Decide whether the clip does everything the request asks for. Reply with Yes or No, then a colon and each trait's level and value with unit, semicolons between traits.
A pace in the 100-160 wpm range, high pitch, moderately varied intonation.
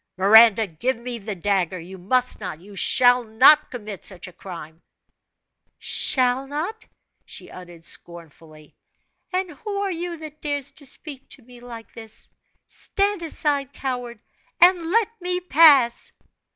No: average, 140 wpm; high, 245 Hz; wide, 7.7 semitones